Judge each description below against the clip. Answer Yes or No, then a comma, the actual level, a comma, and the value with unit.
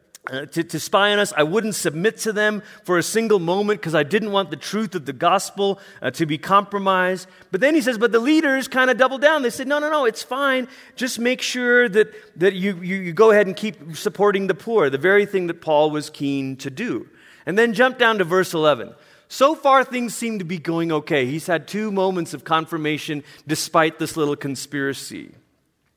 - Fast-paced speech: Yes, fast, 220 wpm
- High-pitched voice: Yes, high, 195 Hz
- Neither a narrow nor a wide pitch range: No, wide, 6.0 semitones